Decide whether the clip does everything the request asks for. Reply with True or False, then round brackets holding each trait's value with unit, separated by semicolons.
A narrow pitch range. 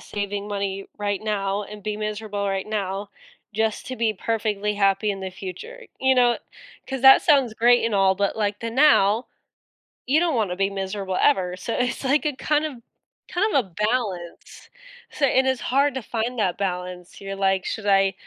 False (4.2 semitones)